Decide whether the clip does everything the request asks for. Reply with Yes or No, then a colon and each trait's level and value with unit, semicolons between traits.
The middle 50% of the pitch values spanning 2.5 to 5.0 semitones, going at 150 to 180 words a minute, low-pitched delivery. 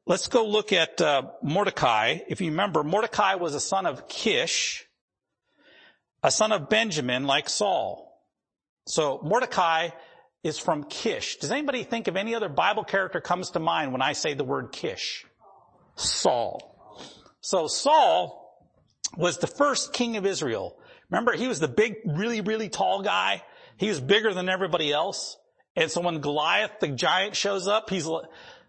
No: average, 4.3 semitones; average, 160 wpm; high, 195 Hz